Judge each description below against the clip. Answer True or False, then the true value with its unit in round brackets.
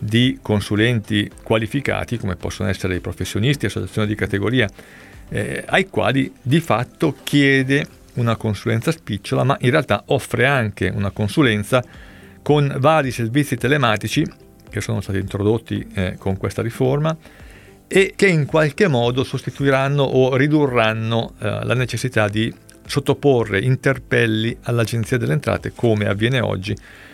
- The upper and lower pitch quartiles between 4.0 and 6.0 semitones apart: True (4.5 semitones)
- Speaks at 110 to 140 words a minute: True (130 wpm)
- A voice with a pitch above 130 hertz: False (115 Hz)